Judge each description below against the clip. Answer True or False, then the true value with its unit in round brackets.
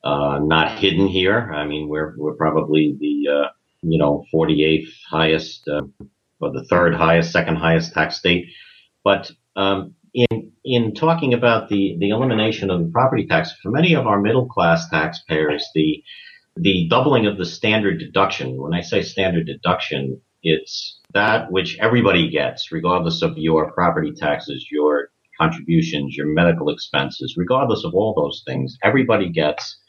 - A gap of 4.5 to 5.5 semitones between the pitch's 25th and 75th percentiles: True (5.0 semitones)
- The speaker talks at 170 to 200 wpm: False (155 wpm)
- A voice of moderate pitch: False (85 Hz)